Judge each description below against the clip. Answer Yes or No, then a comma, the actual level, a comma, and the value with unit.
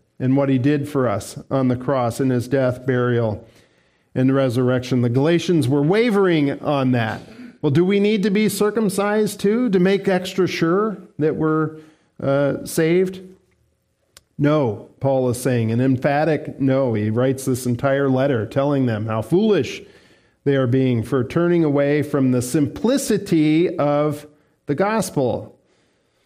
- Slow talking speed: No, average, 150 wpm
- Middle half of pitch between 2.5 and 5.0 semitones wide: No, wide, 5.4 semitones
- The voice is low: No, medium, 145 Hz